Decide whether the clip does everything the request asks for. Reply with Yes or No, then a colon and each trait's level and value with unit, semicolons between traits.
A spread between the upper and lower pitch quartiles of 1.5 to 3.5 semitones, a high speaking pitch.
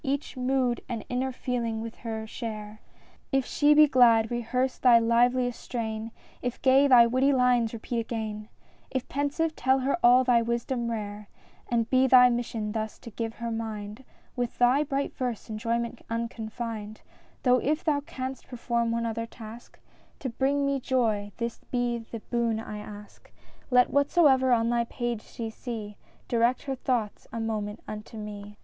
Yes: narrow, 2.4 semitones; high, 235 Hz